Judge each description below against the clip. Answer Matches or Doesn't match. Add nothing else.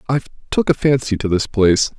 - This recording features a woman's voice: Doesn't match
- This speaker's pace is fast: Matches